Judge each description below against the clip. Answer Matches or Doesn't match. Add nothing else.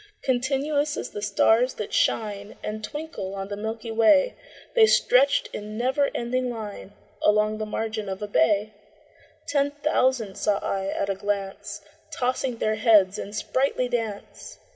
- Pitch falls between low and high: Doesn't match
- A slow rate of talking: Doesn't match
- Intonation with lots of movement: Doesn't match